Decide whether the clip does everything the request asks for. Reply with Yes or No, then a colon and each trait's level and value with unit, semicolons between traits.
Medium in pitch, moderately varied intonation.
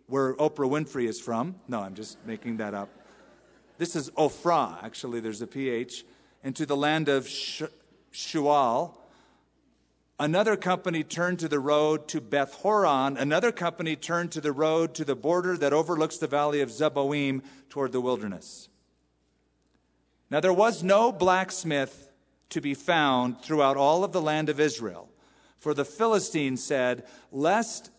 Yes: medium, 145 Hz; average, 3.9 semitones